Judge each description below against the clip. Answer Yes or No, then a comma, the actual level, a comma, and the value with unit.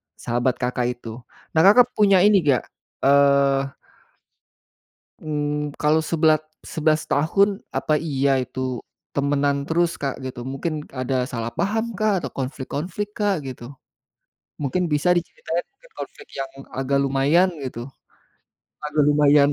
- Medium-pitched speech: Yes, medium, 145 Hz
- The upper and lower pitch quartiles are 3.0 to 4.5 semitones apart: Yes, average, 4.1 semitones